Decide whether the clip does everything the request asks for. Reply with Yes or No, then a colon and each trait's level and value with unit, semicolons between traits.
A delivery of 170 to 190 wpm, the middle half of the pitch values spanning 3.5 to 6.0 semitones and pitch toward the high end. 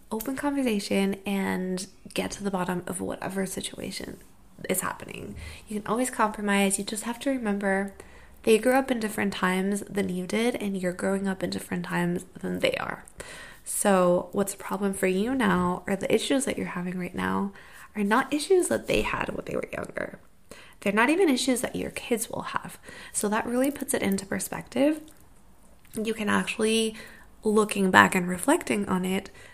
Yes: average, 185 wpm; average, 3.8 semitones; high, 205 Hz